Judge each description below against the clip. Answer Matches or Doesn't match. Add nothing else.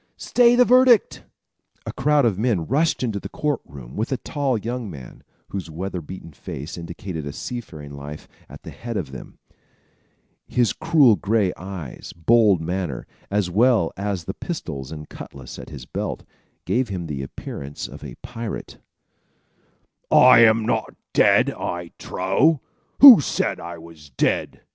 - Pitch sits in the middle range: Doesn't match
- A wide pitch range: Matches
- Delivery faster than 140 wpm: Matches